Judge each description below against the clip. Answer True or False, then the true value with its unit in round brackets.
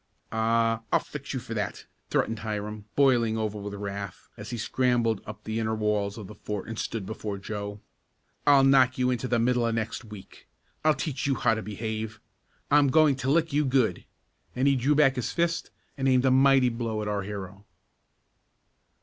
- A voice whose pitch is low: True (115 Hz)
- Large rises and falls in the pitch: False (3.7 semitones)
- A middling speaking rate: True (190 wpm)